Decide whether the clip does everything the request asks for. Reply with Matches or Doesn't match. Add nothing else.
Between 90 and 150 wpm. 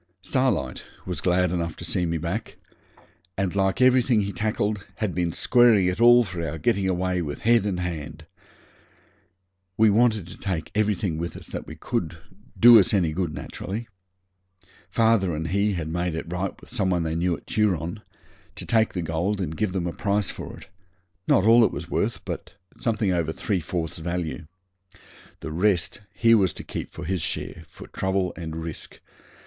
Doesn't match